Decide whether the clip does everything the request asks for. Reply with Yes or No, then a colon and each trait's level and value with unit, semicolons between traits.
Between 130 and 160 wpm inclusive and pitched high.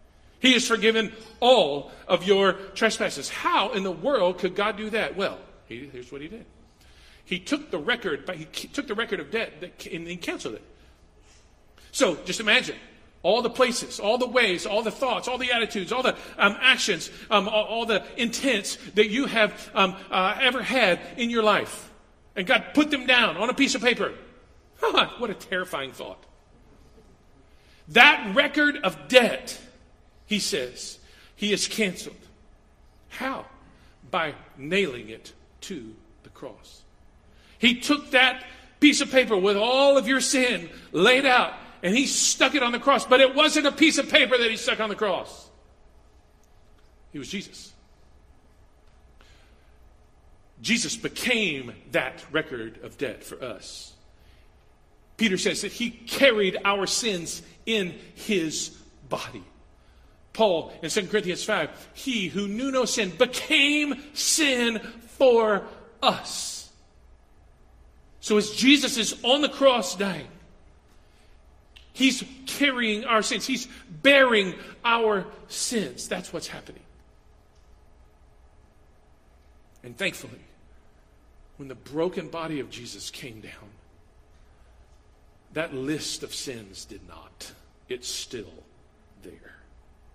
Yes: average, 140 wpm; high, 205 Hz